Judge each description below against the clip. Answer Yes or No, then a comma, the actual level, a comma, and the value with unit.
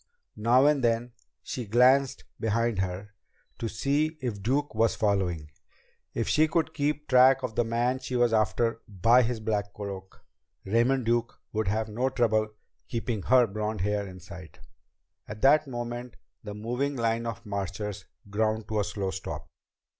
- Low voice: Yes, low, 115 Hz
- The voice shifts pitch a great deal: No, average, 3.3 semitones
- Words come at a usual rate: Yes, average, 160 wpm